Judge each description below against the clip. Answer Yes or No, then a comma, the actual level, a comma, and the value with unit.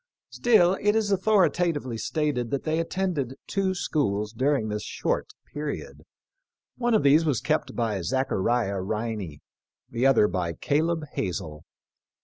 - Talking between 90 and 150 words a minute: Yes, average, 140 wpm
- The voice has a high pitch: No, medium, 140 Hz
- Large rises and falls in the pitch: Yes, wide, 7.9 semitones